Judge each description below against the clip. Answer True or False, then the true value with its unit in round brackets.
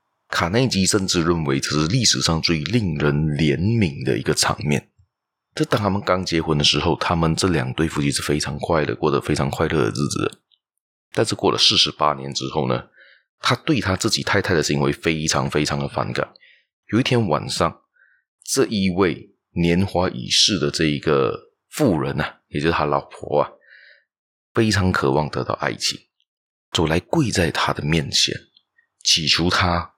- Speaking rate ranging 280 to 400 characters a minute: False (250 characters per minute)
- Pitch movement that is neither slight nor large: True (4.2 semitones)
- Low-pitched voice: True (80 Hz)